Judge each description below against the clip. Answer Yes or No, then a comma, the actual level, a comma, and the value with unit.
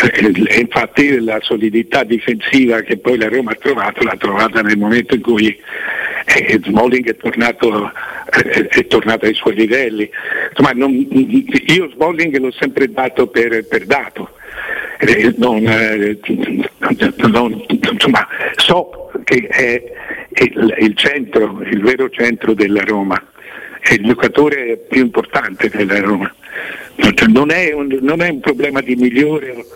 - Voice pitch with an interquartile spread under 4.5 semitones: No, average, 4.9 semitones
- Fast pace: No, average, 130 wpm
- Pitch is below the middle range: Yes, low, 120 Hz